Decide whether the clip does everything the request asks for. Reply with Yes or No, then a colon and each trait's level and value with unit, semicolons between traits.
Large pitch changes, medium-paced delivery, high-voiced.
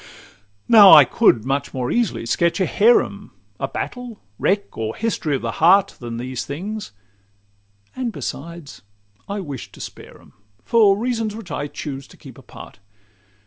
No: wide, 8.0 semitones; average, 155 wpm; medium, 170 Hz